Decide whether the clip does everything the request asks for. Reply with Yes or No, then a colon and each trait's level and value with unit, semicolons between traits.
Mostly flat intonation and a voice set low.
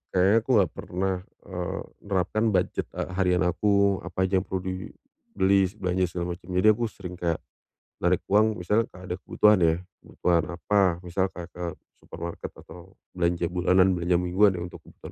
Yes: narrow, 2.0 semitones; very low, 90 Hz